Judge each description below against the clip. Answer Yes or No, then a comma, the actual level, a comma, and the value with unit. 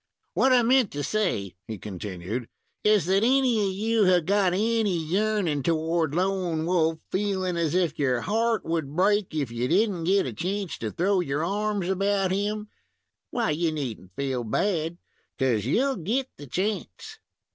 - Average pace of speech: Yes, average, 170 wpm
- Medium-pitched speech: Yes, medium, 180 Hz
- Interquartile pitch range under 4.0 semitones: No, wide, 5.4 semitones